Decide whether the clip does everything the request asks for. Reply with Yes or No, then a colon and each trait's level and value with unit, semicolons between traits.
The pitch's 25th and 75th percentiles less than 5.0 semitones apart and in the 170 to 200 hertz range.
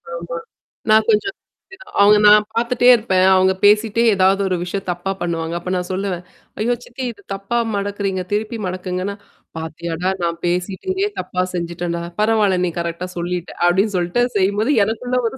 Yes: average, 3.3 semitones; high, 190 Hz